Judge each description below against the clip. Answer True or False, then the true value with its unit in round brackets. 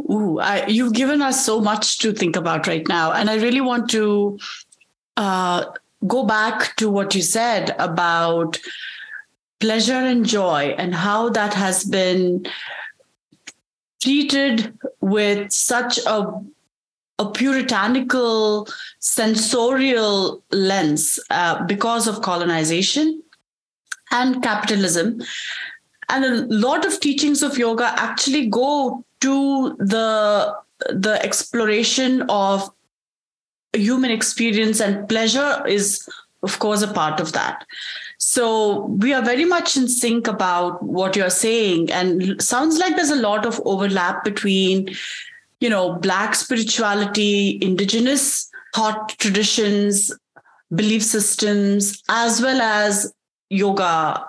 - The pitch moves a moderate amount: True (4.3 semitones)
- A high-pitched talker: True (220 Hz)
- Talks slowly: True (115 wpm)